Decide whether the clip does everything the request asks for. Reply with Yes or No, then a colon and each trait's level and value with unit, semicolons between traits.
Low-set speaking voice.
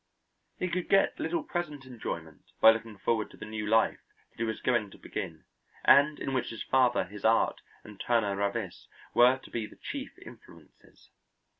Yes: low, 115 Hz